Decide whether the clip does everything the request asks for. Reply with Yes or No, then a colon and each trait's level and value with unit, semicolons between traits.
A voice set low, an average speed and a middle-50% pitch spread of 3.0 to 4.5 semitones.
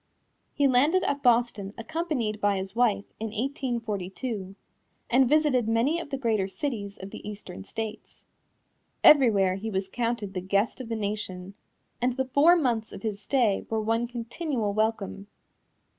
No: high, 225 Hz; average, 155 wpm; average, 4.1 semitones